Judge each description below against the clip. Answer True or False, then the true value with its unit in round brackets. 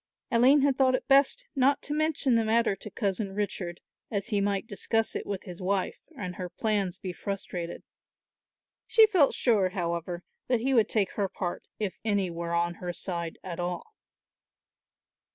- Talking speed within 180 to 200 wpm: False (170 wpm)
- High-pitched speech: True (200 Hz)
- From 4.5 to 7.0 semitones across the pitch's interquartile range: True (5.0 semitones)